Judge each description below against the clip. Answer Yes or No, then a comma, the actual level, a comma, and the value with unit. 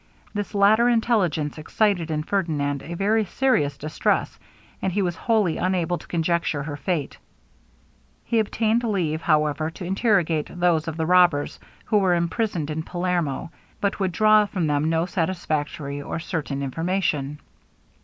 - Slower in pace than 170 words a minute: Yes, average, 145 wpm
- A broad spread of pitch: No, average, 4.5 semitones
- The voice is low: No, medium, 170 Hz